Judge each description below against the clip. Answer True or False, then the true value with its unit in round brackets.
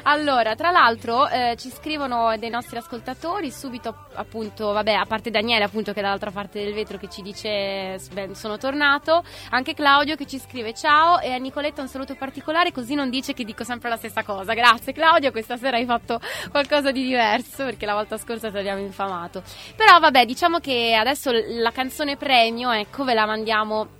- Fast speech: True (195 wpm)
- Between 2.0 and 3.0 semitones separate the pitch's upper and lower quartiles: False (4.2 semitones)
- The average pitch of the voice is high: True (240 Hz)